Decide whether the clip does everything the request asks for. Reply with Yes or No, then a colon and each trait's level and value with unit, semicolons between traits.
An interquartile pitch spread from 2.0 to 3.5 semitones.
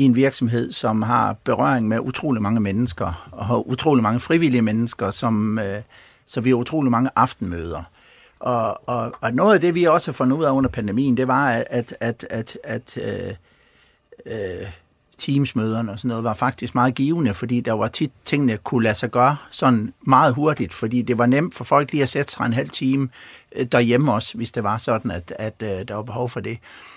Yes: average, 2.9 semitones